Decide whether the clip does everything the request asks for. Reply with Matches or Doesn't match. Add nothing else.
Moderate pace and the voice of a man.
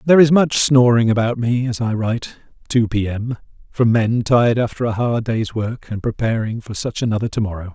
Doesn't match